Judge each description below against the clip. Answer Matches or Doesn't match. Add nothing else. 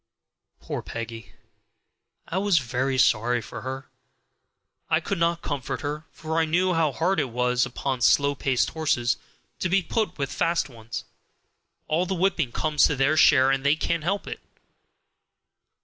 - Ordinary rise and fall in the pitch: Matches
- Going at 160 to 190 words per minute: Matches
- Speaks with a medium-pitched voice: Matches